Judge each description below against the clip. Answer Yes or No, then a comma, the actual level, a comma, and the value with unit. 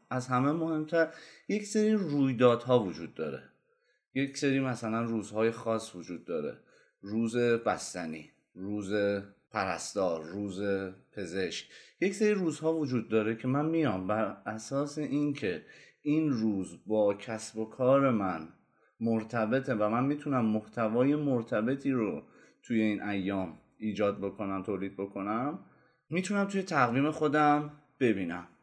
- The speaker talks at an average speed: Yes, average, 120 wpm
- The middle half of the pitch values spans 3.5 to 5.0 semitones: No, wide, 5.6 semitones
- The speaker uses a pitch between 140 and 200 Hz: No, low, 115 Hz